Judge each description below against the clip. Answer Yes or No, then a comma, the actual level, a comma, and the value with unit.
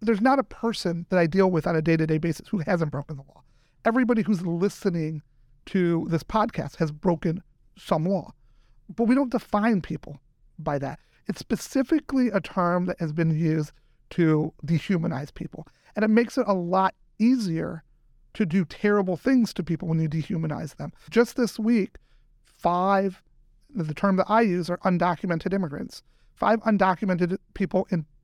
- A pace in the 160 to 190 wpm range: Yes, average, 170 wpm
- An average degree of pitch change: Yes, average, 4.5 semitones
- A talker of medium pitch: Yes, medium, 180 Hz